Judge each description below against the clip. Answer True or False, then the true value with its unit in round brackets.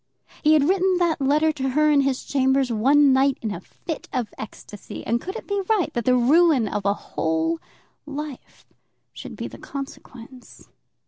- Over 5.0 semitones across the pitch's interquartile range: False (4.3 semitones)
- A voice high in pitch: True (275 Hz)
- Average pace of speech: True (180 wpm)